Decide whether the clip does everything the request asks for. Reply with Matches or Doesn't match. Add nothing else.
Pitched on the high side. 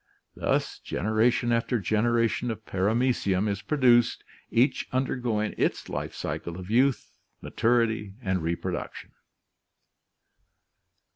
Doesn't match